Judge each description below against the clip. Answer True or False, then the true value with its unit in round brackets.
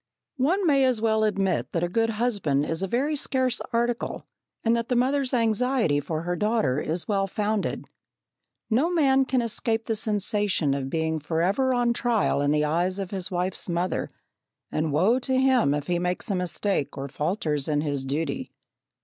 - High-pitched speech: True (205 Hz)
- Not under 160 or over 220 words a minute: True (180 wpm)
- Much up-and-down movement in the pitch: True (6.9 semitones)